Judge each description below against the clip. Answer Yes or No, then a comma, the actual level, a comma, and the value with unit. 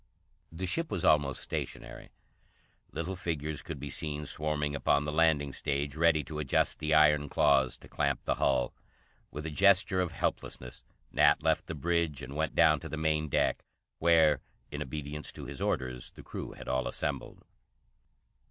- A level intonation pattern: Yes, narrow, 2.1 semitones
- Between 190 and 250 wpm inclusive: No, average, 170 wpm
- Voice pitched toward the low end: Yes, very low, 75 Hz